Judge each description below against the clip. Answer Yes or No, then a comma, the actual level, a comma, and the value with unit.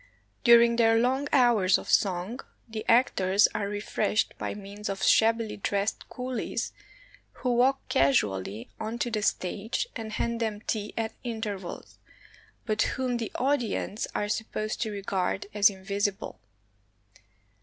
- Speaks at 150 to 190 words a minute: No, slow, 135 wpm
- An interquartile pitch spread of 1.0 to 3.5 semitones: Yes, average, 2.8 semitones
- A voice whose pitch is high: Yes, high, 215 Hz